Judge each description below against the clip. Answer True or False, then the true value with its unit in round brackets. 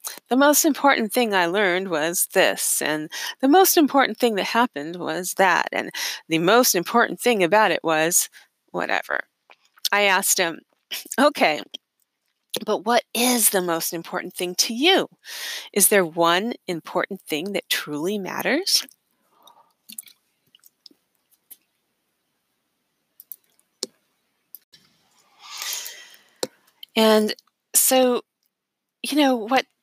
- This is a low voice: False (220 Hz)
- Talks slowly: True (105 wpm)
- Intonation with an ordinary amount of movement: False (6.9 semitones)